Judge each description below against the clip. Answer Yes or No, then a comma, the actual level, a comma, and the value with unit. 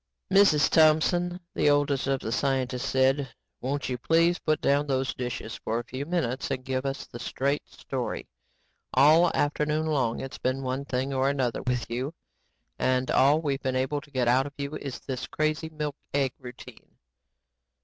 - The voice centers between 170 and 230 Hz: No, low, 135 Hz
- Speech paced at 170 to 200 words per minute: Yes, average, 175 wpm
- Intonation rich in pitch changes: No, narrow, 2.6 semitones